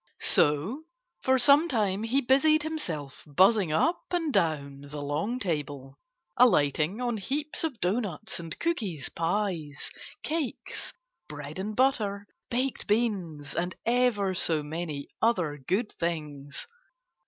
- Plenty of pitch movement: Yes, wide, 8.5 semitones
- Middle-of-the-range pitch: No, high, 195 Hz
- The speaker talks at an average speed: No, slow, 120 wpm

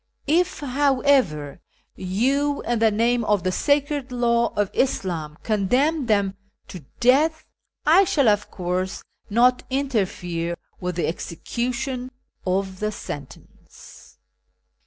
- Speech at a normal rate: No, slow, 115 wpm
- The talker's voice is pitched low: No, high, 235 Hz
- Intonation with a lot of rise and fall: Yes, wide, 6.3 semitones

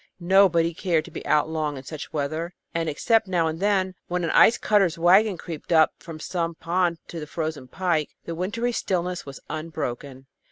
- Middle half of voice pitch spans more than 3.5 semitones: No, average, 2.9 semitones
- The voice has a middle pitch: Yes, medium, 165 Hz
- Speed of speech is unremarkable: Yes, average, 190 wpm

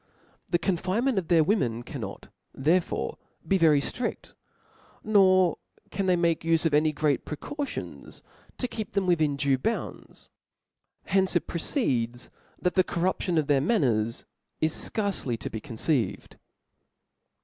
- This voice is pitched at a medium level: Yes, medium, 165 Hz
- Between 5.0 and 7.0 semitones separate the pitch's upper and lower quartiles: Yes, average, 5.3 semitones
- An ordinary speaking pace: Yes, average, 150 wpm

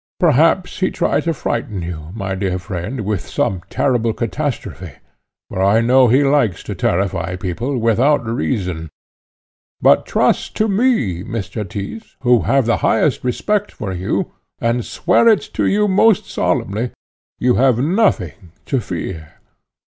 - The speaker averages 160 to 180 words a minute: No, average, 145 wpm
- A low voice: Yes, low, 115 Hz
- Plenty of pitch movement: Yes, wide, 7.1 semitones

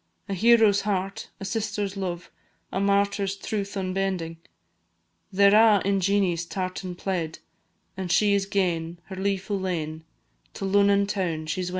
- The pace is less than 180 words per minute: Yes, average, 155 wpm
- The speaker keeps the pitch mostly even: Yes, narrow, 1.8 semitones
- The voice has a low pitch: No, high, 195 Hz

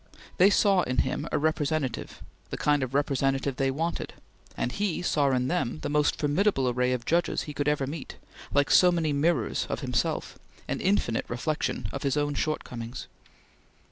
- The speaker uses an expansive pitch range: No, average, 3.3 semitones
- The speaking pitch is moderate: Yes, medium, 145 Hz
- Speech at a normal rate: Yes, average, 170 wpm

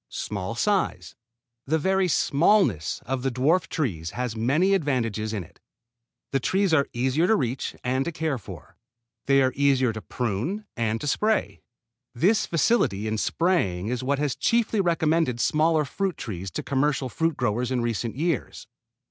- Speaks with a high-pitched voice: No, low, 135 Hz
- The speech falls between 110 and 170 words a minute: Yes, average, 160 wpm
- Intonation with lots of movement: Yes, wide, 6.2 semitones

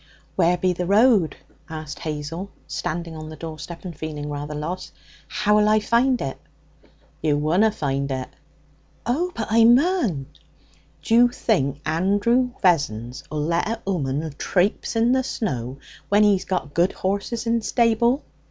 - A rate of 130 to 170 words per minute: Yes, average, 145 wpm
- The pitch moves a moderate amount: No, wide, 6.8 semitones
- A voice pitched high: No, medium, 180 Hz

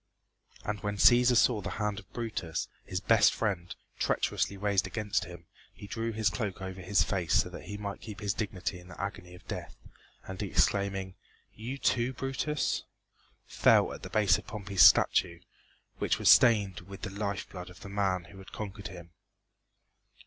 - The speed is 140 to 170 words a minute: No, average, 180 wpm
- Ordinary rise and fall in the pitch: No, narrow, 2.3 semitones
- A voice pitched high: No, low, 100 Hz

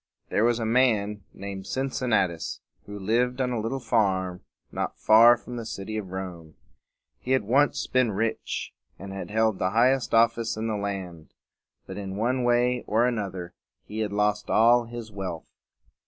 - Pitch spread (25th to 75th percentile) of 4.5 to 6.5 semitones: No, average, 3.5 semitones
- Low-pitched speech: Yes, low, 110 Hz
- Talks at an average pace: Yes, average, 175 wpm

